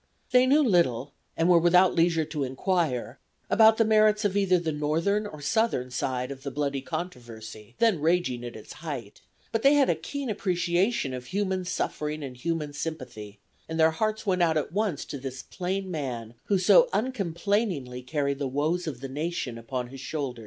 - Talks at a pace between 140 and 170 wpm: No, average, 185 wpm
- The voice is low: No, medium, 160 Hz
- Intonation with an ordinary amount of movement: No, wide, 6.4 semitones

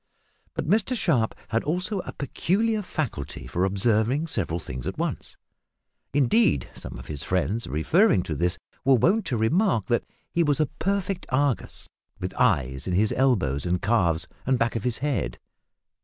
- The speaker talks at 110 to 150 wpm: No, average, 165 wpm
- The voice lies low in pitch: Yes, low, 120 Hz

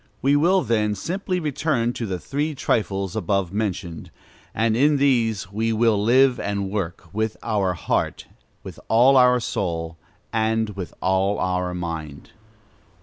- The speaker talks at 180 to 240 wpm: No, average, 145 wpm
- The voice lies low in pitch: Yes, low, 110 Hz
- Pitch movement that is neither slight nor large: Yes, average, 4.8 semitones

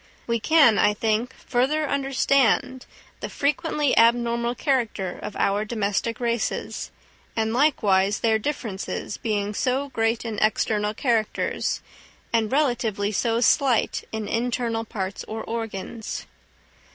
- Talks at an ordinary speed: No, slow, 115 wpm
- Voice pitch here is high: Yes, high, 230 Hz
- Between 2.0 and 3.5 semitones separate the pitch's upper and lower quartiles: Yes, average, 2.9 semitones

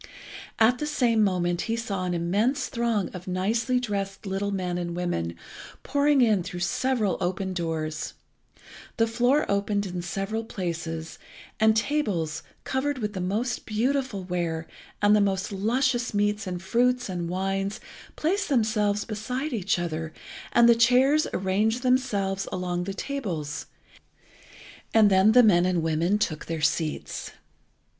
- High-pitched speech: Yes, high, 200 Hz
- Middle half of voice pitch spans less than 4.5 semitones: No, average, 4.9 semitones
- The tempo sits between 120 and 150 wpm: Yes, average, 145 wpm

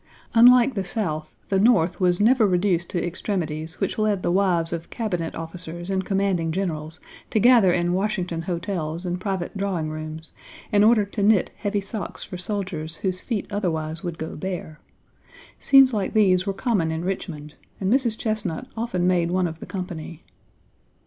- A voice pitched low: No, medium, 185 Hz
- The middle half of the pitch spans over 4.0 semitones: No, average, 3.6 semitones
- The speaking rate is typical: Yes, average, 170 wpm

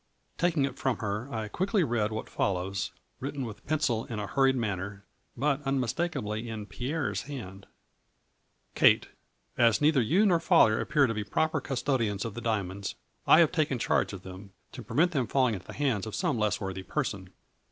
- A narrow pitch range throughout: No, wide, 5.6 semitones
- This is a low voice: Yes, low, 115 Hz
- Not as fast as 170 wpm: No, average, 190 wpm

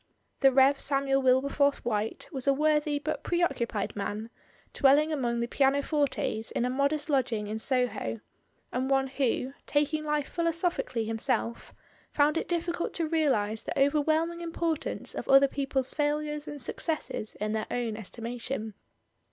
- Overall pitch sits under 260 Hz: No, very high, 275 Hz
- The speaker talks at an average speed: Yes, average, 150 wpm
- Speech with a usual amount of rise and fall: Yes, average, 4.1 semitones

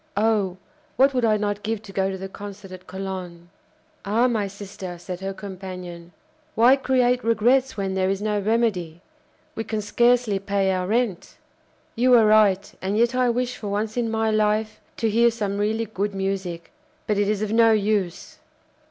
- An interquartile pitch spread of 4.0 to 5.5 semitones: No, average, 2.8 semitones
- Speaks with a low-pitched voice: No, high, 210 Hz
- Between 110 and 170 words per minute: No, average, 180 wpm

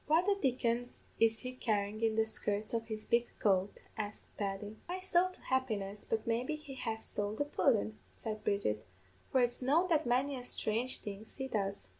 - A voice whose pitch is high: Yes, high, 225 Hz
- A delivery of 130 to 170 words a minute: No, average, 190 wpm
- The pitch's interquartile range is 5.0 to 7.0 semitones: No, average, 3.8 semitones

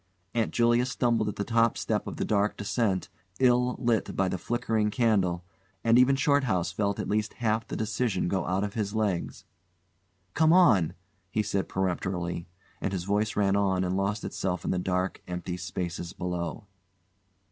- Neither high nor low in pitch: No, low, 100 Hz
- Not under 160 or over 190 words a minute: Yes, average, 170 wpm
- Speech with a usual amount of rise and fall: Yes, average, 3.8 semitones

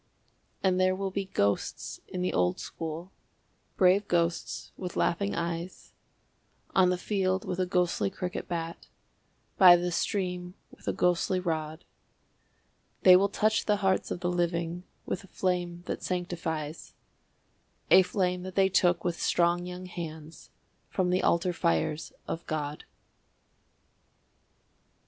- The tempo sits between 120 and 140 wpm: Yes, slow, 135 wpm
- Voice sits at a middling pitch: Yes, medium, 180 Hz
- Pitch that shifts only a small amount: Yes, narrow, 1.7 semitones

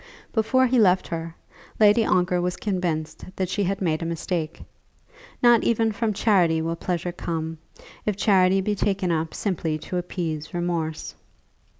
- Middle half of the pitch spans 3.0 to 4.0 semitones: Yes, average, 3.7 semitones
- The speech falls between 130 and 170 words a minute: Yes, average, 155 wpm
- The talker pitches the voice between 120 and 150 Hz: No, medium, 180 Hz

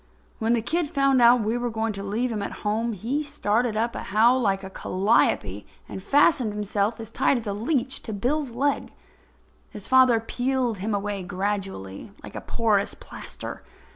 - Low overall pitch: No, high, 225 Hz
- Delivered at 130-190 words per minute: Yes, average, 180 wpm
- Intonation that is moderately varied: Yes, average, 3.6 semitones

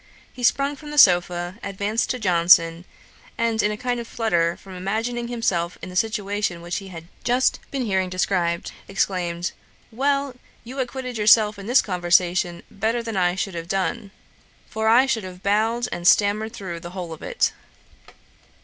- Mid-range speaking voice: No, high, 200 Hz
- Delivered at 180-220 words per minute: No, average, 170 wpm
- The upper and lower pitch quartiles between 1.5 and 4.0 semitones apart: No, average, 4.6 semitones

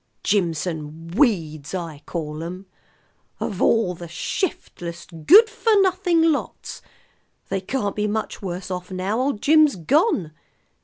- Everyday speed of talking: No, slow, 125 wpm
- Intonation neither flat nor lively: No, wide, 9.0 semitones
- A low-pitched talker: No, high, 190 Hz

